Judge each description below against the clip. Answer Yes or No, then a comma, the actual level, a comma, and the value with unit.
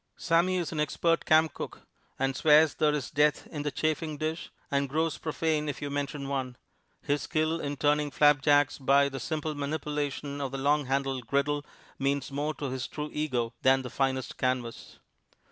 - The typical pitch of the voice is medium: Yes, medium, 145 Hz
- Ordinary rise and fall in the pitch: No, narrow, 2.0 semitones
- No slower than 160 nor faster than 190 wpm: Yes, average, 180 wpm